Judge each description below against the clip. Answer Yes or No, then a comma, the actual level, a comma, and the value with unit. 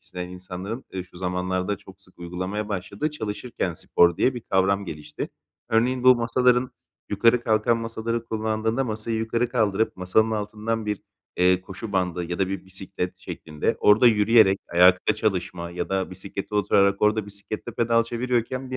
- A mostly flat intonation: No, average, 3.7 semitones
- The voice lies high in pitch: No, low, 105 Hz